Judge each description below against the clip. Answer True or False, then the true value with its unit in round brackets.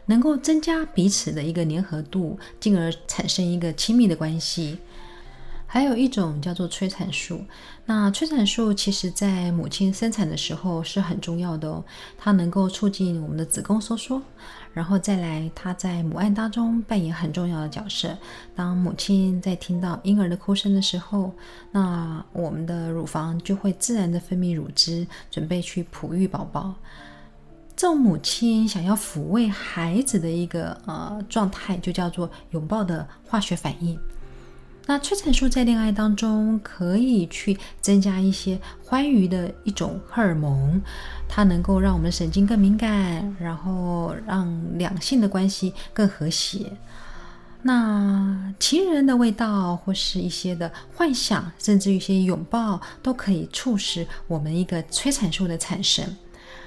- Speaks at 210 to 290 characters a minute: True (235 characters per minute)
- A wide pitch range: False (3.3 semitones)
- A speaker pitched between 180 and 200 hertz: True (190 Hz)